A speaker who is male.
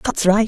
No: female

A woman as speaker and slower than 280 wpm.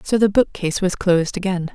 Yes: female; fast, 205 wpm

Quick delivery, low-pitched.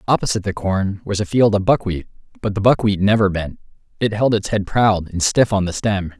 Yes: fast, 225 wpm; low, 100 Hz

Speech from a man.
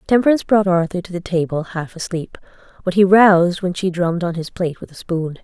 No: female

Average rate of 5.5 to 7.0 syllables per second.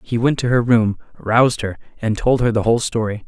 Yes: 5.7 syllables/s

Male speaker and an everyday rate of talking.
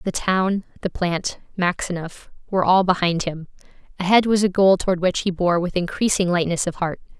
No: female; average, 185 wpm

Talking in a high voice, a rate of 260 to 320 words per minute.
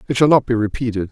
No: low, 120 Hz; fast, 270 wpm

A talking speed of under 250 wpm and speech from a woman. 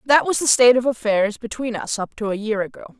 No: fast, 260 wpm; female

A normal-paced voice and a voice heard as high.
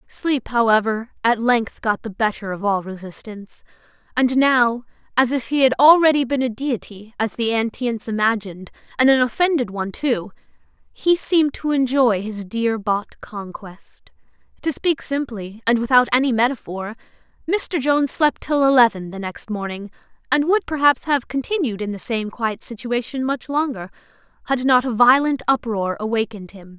Yes: average, 155 wpm; high, 240 Hz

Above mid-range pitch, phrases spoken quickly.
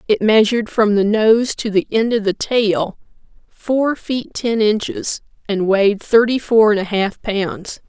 No: high, 215 Hz; average, 175 wpm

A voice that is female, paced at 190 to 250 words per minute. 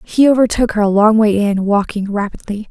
Yes: female; average, 200 wpm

